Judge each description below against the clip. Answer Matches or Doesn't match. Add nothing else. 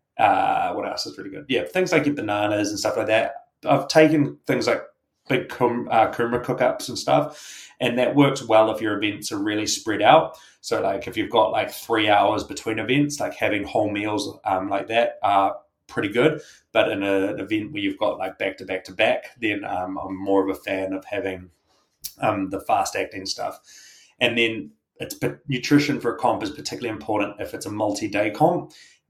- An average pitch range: Doesn't match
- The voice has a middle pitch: Doesn't match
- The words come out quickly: Matches